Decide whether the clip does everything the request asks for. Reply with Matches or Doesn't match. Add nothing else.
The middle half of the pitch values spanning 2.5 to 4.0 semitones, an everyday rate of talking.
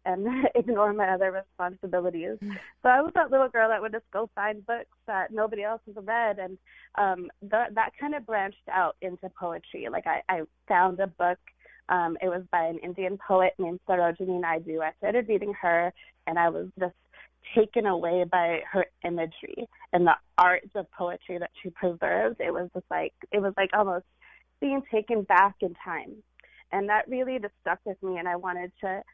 Matches